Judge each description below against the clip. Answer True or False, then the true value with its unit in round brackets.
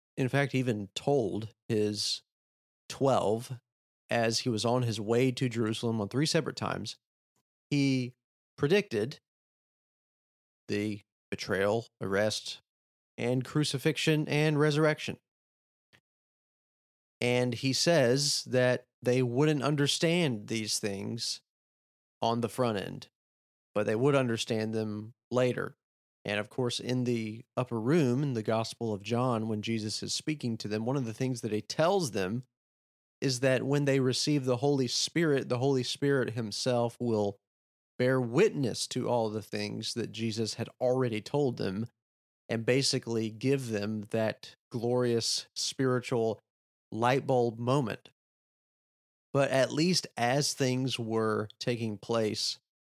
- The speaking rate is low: True (130 wpm)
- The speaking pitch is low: True (120 Hz)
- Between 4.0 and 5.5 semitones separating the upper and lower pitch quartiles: False (3.5 semitones)